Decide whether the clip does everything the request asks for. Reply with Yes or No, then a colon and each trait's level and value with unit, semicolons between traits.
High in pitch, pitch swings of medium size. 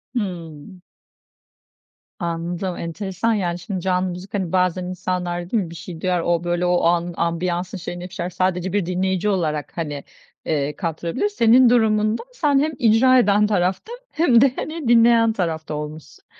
No: medium, 180 Hz; average, 3.8 semitones